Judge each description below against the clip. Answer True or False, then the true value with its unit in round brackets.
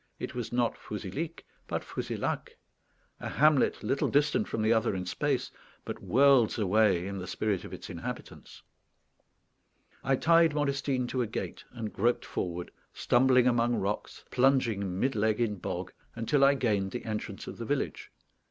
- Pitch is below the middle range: True (120 Hz)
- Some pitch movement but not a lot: True (4.6 semitones)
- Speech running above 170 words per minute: False (160 wpm)